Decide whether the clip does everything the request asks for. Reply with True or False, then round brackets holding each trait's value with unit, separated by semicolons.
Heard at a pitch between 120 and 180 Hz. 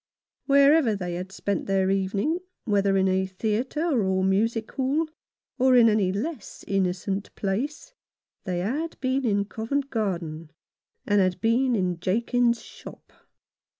False (210 Hz)